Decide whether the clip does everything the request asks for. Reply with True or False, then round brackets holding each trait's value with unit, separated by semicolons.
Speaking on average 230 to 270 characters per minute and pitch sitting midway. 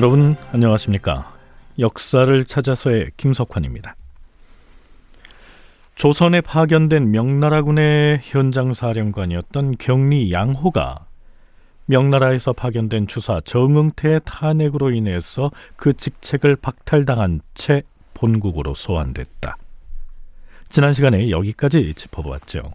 False (260 characters per minute; 120 Hz)